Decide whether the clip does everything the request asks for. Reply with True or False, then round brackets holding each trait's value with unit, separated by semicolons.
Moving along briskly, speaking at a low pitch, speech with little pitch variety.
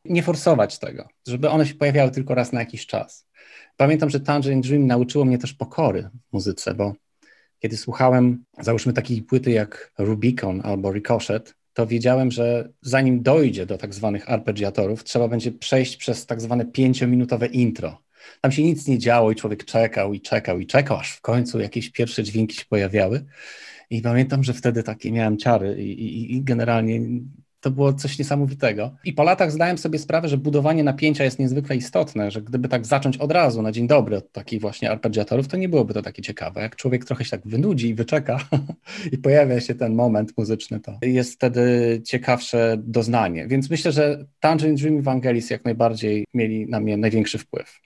False (185 wpm; 120 Hz; 3.5 semitones)